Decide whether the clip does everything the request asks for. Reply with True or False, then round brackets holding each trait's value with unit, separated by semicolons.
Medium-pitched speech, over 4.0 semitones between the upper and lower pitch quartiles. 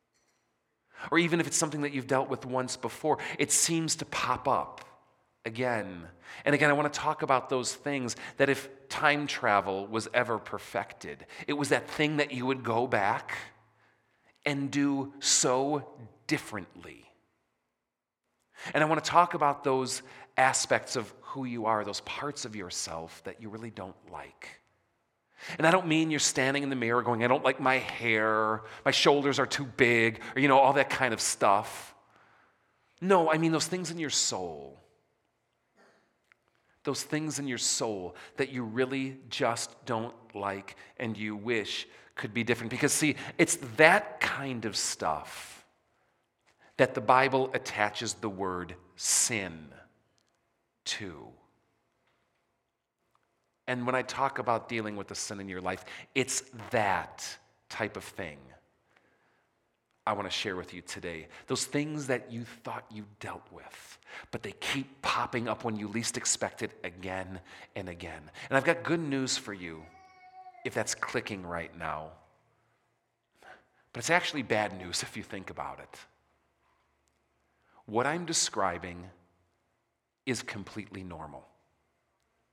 False (120 Hz; 5.2 semitones)